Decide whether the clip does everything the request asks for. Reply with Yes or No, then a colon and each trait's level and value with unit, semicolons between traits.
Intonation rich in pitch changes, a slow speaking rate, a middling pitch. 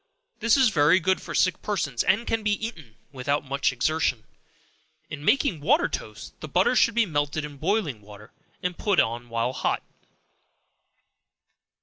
No: wide, 8.1 semitones; average, 155 wpm; medium, 155 Hz